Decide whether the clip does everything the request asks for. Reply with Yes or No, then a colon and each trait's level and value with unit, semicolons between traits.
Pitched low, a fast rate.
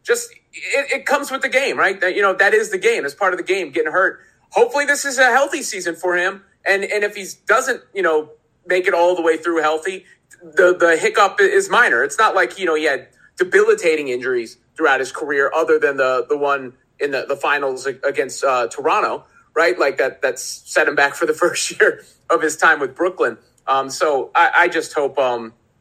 No: high, 195 Hz; fast, 225 wpm